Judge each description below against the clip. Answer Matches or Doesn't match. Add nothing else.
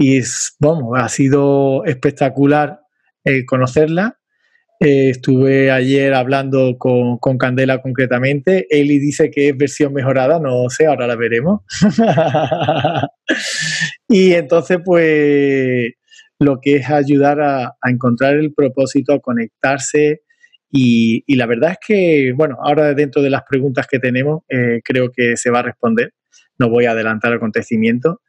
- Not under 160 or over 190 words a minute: Doesn't match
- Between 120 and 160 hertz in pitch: Matches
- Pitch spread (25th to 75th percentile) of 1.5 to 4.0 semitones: Matches